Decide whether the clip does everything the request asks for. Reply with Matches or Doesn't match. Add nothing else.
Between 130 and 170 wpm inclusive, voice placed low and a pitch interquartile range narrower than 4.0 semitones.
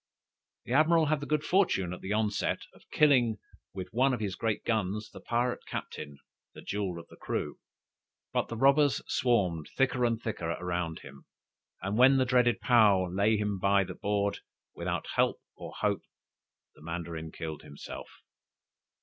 Doesn't match